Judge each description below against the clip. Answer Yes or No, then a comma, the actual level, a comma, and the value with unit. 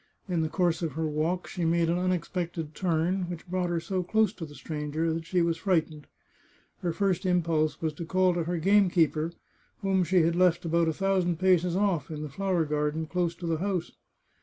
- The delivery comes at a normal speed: No, fast, 210 wpm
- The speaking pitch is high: No, medium, 170 Hz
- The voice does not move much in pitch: Yes, narrow, 2.2 semitones